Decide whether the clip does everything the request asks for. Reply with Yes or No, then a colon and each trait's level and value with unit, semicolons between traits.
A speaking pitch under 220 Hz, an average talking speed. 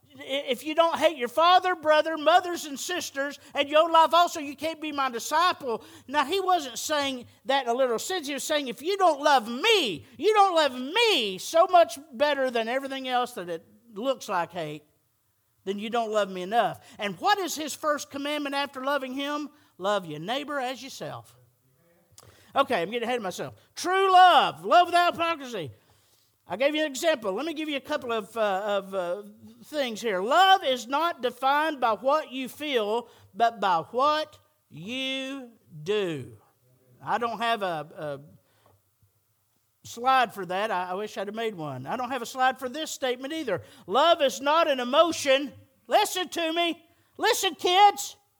No: very high, 265 Hz; average, 180 wpm